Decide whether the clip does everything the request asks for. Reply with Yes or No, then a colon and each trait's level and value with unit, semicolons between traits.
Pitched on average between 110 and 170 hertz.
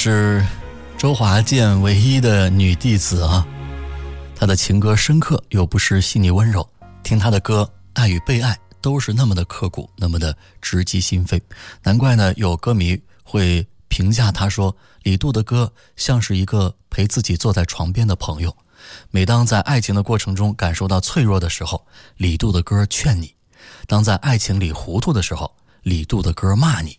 No: low, 100 Hz